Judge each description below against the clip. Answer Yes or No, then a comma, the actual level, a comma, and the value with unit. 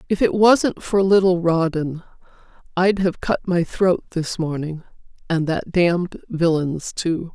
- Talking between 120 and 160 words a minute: Yes, average, 140 wpm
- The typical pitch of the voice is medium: Yes, medium, 175 Hz